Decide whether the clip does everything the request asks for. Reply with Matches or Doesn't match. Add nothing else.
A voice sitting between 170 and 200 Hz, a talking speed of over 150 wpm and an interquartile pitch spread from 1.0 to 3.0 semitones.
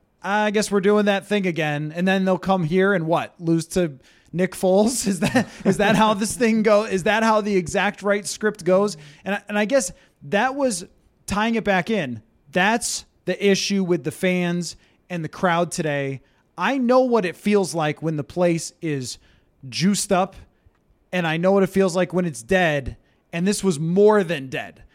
Doesn't match